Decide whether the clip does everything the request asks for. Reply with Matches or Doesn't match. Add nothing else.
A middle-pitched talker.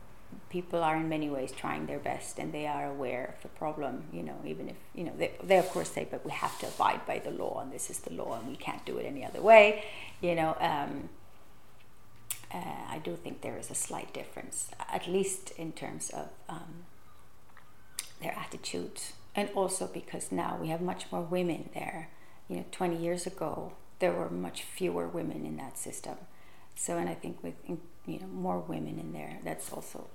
Matches